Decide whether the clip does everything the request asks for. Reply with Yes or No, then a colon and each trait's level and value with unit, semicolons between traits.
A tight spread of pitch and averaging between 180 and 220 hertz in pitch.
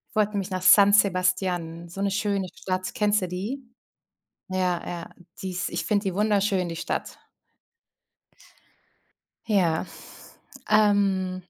Yes: narrow, 2.0 semitones; high, 190 Hz